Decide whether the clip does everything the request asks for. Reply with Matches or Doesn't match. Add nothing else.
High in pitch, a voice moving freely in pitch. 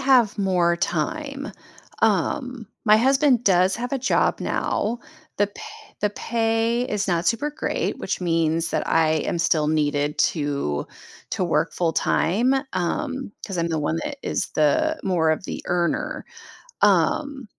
Matches